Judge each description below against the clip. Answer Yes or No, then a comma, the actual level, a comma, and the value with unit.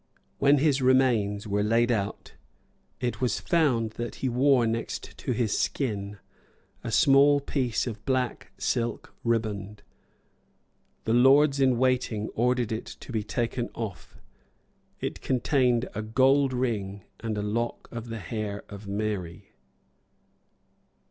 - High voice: No, low, 115 Hz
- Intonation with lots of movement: No, average, 3.5 semitones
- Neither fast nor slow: No, slow, 130 wpm